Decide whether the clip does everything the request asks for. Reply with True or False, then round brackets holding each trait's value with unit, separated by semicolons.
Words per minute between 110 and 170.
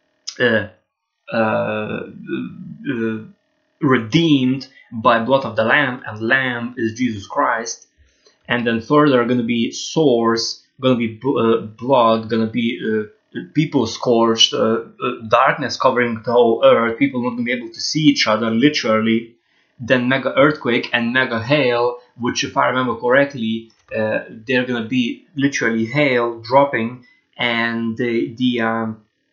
True (140 wpm)